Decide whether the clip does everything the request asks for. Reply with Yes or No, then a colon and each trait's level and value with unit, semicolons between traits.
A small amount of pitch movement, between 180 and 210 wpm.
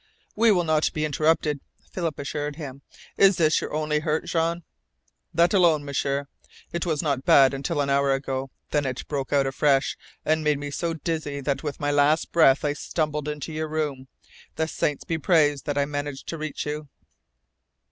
Yes: narrow, 2.1 semitones; average, 185 wpm